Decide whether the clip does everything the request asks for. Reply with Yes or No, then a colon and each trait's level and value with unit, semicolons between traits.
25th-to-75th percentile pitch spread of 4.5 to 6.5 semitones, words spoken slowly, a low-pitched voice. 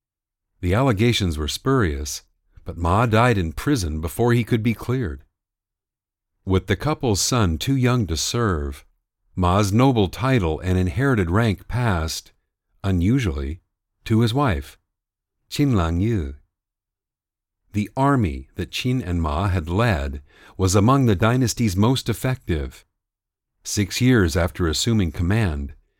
Yes: wide, 5.4 semitones; slow, 125 wpm; low, 100 Hz